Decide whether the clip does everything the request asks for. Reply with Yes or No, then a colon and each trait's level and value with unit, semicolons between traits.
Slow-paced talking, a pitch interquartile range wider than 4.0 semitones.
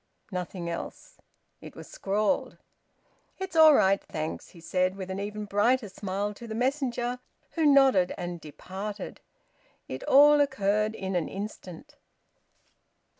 Yes: slow, 130 wpm; wide, 5.6 semitones